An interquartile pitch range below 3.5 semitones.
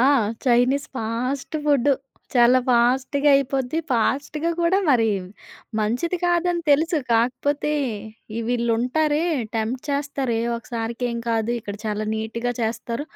No: average, 3.8 semitones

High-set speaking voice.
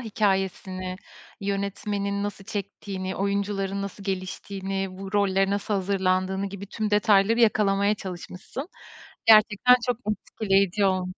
Yes: high, 200 Hz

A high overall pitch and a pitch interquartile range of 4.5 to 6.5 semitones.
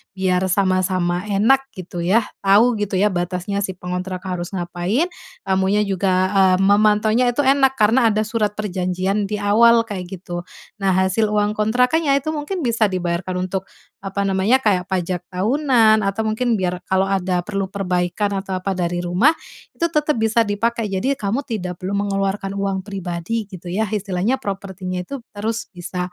No: high, 195 Hz; average, 3.1 semitones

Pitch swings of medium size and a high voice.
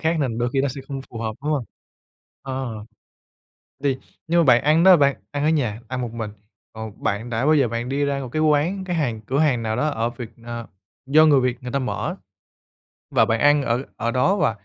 No: average, 4.1 semitones; low, 130 Hz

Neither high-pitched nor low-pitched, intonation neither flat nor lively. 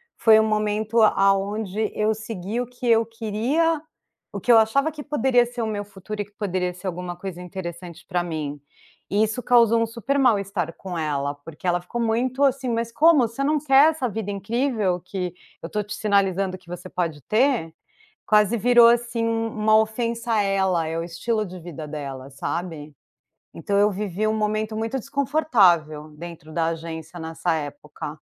No: high, 210 Hz; average, 4.7 semitones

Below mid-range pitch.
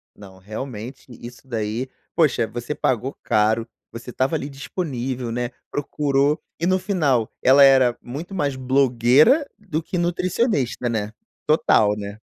Yes: low, 130 Hz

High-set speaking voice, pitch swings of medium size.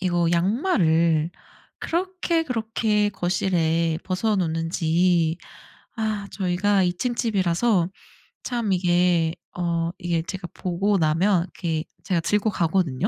No: medium, 180 Hz; average, 3.7 semitones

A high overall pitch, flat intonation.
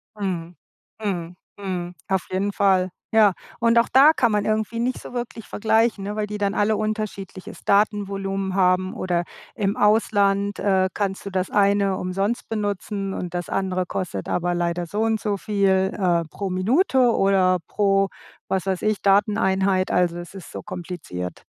Yes: high, 195 Hz; narrow, 2.2 semitones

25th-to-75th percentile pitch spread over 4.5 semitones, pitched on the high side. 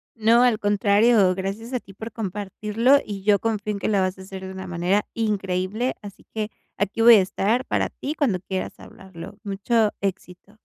No: average, 2.8 semitones; high, 205 Hz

